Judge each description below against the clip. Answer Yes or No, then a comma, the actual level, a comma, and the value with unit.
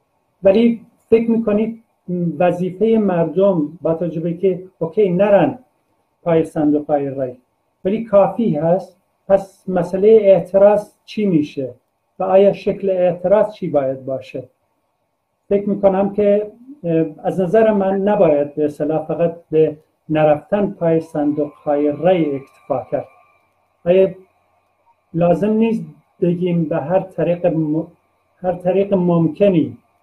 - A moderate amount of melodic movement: Yes, average, 4.1 semitones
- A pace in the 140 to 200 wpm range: No, average, 115 wpm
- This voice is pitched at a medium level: Yes, medium, 180 Hz